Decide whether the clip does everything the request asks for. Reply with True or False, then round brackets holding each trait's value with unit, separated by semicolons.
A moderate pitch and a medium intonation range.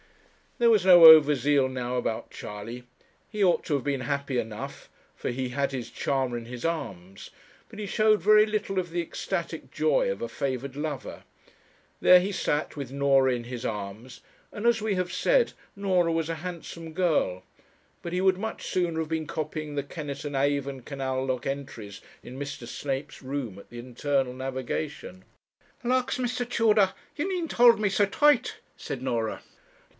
False (145 Hz; 6.5 semitones)